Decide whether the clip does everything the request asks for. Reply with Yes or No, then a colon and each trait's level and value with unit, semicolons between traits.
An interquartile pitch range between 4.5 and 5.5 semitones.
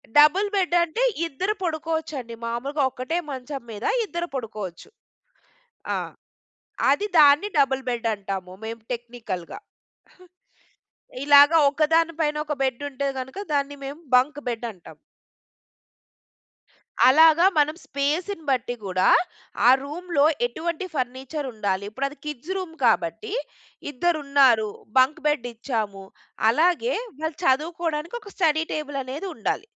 Yes: average, 4.8 semitones